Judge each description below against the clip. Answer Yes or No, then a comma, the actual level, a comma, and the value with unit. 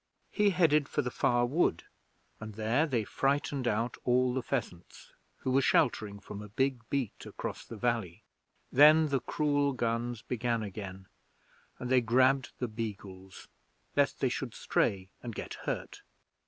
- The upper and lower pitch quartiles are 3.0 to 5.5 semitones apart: Yes, average, 4.0 semitones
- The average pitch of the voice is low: Yes, low, 120 Hz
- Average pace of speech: Yes, average, 150 wpm